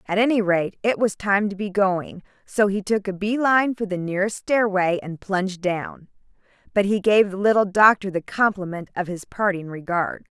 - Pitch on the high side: Yes, high, 195 Hz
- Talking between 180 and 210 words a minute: Yes, average, 195 wpm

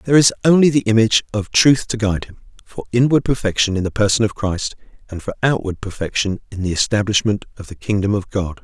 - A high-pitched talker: No, low, 105 Hz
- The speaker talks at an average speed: No, fast, 210 wpm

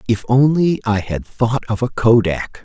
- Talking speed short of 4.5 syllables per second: Yes, 4.2 syllables/s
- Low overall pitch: Yes, low, 115 Hz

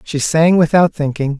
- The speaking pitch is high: No, medium, 155 Hz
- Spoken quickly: No, average, 170 wpm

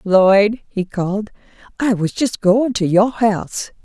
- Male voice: No, female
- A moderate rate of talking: Yes, average, 155 wpm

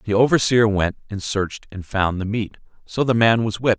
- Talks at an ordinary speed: No, fast, 220 wpm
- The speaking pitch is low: Yes, low, 105 Hz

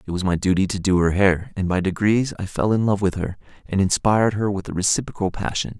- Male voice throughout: Yes, male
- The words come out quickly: Yes, fast, 250 wpm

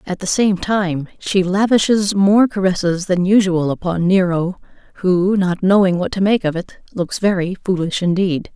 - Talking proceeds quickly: No, average, 170 wpm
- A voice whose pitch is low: No, medium, 185 Hz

